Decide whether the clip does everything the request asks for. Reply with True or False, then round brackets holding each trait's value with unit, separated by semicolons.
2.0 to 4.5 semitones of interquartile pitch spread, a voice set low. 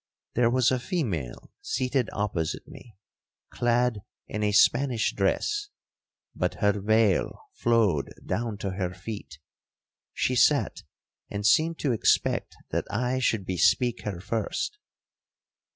True (3.9 semitones; 110 Hz)